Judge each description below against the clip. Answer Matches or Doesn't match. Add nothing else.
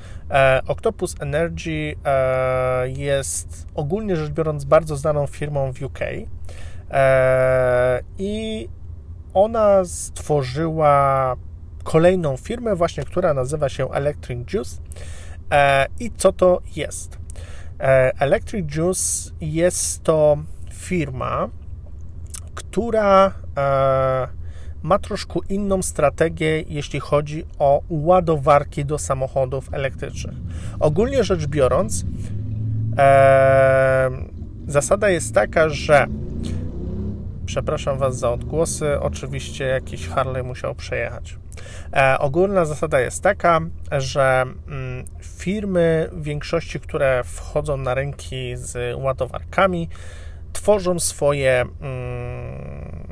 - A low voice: Matches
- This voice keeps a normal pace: Doesn't match